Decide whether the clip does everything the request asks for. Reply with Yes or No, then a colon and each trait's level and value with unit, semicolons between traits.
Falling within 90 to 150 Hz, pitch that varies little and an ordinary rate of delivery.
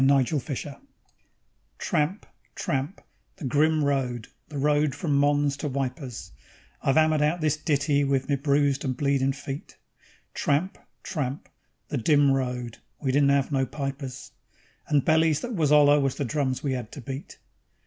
Yes: medium, 140 Hz; narrow, 1.8 semitones; average, 160 wpm